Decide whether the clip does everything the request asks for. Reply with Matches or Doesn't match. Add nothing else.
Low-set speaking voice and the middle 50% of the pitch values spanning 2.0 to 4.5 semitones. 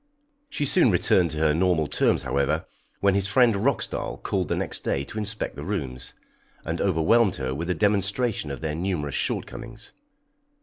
Doesn't match